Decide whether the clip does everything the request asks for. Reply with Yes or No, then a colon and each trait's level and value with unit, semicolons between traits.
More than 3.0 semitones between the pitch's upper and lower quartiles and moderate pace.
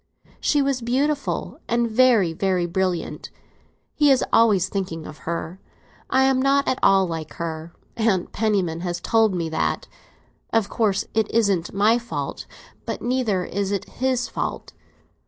Yes: average, 5.3 semitones; average, 150 wpm